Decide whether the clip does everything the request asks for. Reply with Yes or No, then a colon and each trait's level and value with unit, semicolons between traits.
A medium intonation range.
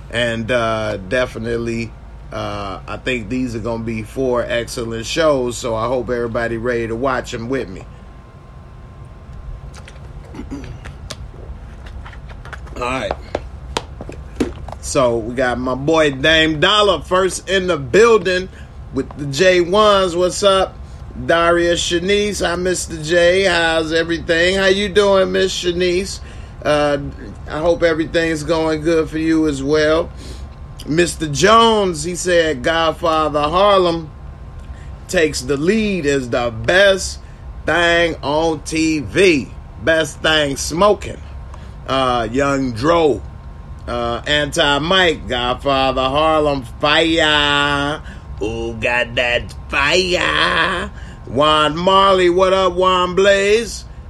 No: wide, 6.5 semitones